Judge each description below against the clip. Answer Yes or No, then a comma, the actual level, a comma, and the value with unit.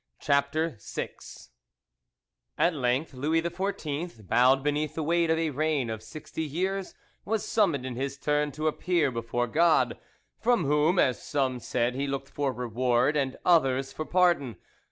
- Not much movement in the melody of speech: No, average, 4.1 semitones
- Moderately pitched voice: Yes, medium, 145 Hz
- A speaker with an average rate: Yes, average, 155 wpm